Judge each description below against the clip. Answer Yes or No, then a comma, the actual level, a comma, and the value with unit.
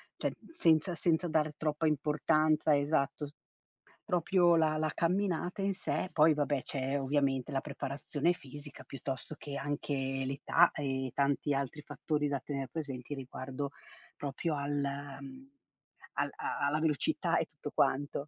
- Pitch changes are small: Yes, narrow, 2.3 semitones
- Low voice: No, medium, 145 Hz